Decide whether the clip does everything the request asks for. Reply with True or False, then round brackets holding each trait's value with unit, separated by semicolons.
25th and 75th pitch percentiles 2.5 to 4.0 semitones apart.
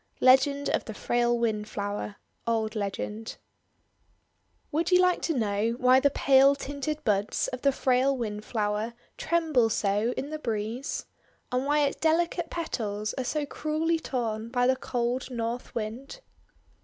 False (4.5 semitones)